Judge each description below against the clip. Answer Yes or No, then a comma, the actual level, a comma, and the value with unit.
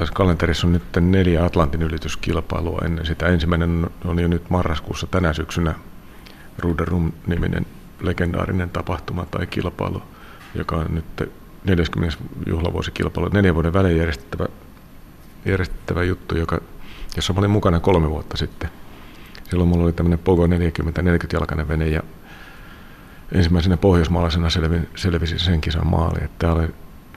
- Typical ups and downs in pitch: No, narrow, 1.4 semitones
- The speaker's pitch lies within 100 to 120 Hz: No, very low, 85 Hz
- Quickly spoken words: No, average, 125 wpm